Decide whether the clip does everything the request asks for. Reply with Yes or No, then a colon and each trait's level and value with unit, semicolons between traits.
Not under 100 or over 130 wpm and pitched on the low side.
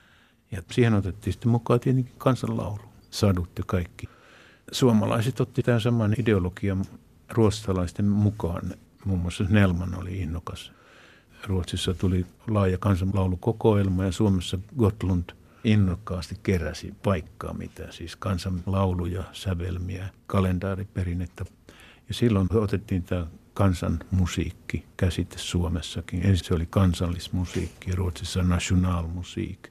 Yes: average, 105 wpm; very low, 95 Hz